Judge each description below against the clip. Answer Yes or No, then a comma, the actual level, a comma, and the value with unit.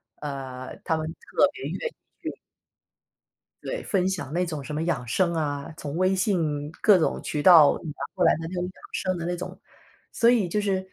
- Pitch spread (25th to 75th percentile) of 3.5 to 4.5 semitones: Yes, average, 4.0 semitones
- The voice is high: No, medium, 170 Hz